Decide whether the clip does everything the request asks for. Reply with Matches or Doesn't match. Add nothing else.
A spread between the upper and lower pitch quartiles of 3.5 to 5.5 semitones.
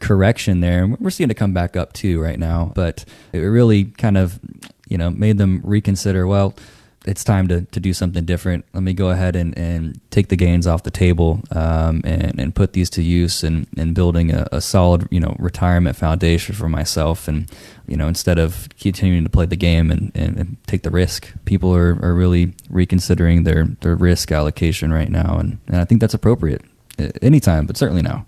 Doesn't match